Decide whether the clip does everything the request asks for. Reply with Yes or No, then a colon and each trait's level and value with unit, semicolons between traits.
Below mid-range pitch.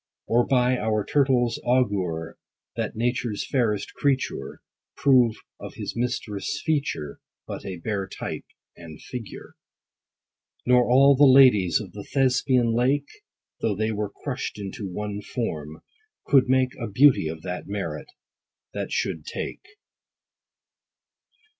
Yes: low, 120 Hz